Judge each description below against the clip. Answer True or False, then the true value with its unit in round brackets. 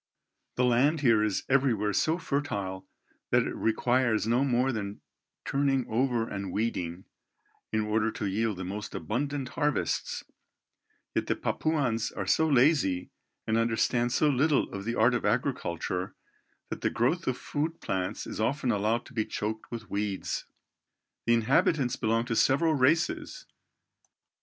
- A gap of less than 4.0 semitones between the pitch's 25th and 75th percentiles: False (4.3 semitones)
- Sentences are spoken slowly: False (145 wpm)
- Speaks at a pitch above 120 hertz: False (115 Hz)